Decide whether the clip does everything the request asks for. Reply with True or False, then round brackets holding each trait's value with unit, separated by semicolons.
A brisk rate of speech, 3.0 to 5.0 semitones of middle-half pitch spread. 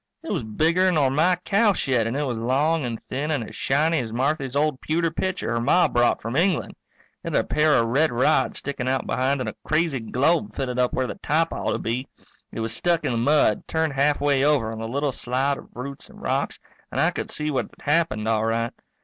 True (230 wpm; 4.3 semitones)